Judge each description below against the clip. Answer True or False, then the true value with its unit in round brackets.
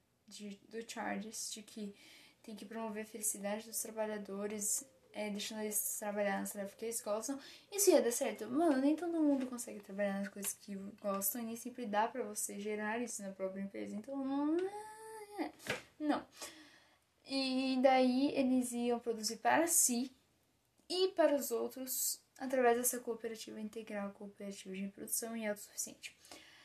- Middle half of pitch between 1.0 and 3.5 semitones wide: False (4.4 semitones)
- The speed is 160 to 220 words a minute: False (150 wpm)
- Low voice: False (230 Hz)